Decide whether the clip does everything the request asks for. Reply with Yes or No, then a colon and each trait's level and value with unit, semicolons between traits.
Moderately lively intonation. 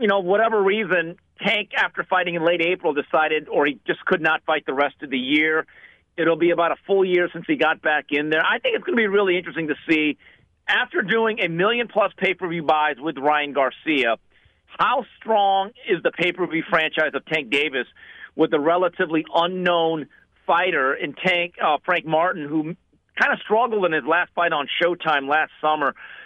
Yes: average, 3.5 semitones